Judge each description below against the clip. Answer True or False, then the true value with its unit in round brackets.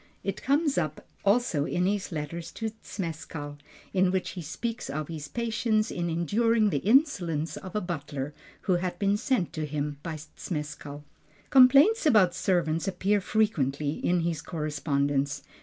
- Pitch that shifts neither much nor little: False (5.8 semitones)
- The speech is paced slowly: False (145 wpm)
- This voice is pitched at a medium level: True (175 Hz)